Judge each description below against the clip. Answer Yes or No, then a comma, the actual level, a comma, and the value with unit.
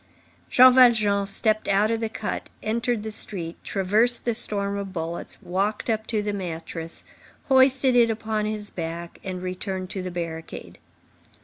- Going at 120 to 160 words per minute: Yes, average, 155 wpm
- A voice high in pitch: Yes, high, 205 Hz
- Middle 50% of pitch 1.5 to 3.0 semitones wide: No, average, 3.4 semitones